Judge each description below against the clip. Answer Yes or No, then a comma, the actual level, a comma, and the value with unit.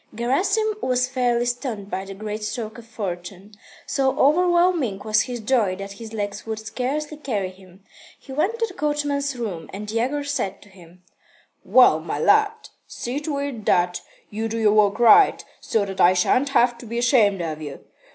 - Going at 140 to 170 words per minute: No, average, 180 wpm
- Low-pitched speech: No, high, 230 Hz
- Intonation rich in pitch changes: Yes, wide, 5.9 semitones